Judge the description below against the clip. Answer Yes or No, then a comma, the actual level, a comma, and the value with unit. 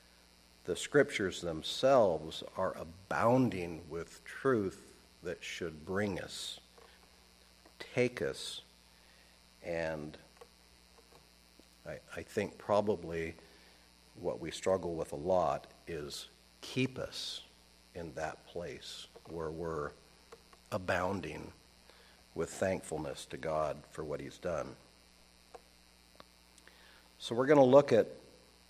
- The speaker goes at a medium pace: No, slow, 100 wpm